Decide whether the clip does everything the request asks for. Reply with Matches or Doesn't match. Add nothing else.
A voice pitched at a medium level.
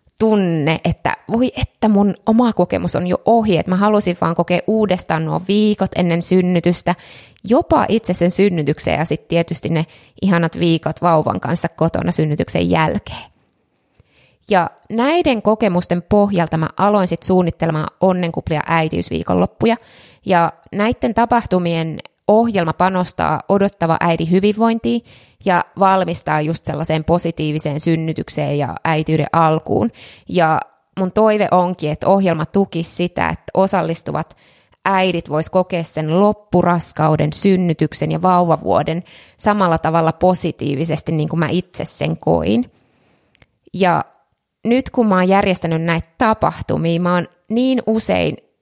Matches